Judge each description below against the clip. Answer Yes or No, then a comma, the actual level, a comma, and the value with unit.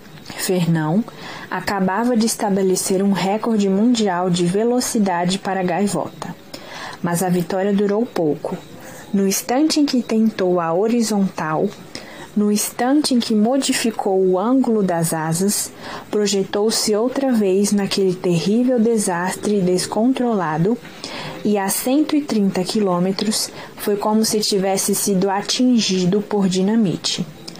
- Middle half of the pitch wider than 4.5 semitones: No, average, 3.2 semitones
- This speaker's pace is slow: Yes, slow, 110 wpm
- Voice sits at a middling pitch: No, high, 200 Hz